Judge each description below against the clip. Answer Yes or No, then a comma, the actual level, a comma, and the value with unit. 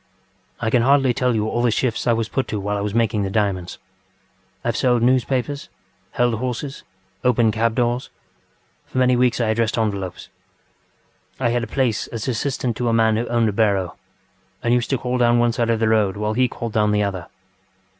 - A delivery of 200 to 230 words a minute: Yes, fast, 205 wpm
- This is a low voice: Yes, low, 115 Hz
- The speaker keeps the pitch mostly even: Yes, narrow, 2.3 semitones